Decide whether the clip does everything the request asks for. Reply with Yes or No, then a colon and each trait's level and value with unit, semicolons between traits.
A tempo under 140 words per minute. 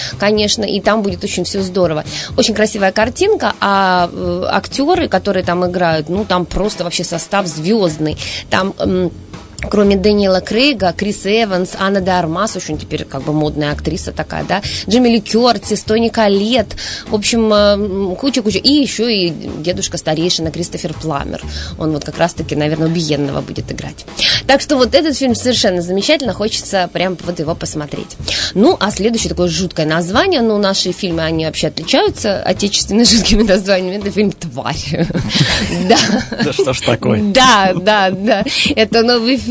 No: average, 155 wpm